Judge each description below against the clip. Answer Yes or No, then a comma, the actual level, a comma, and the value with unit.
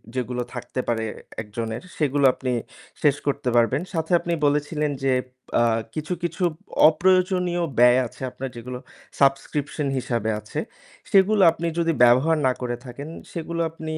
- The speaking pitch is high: No, medium, 145 Hz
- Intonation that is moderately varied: Yes, average, 5.0 semitones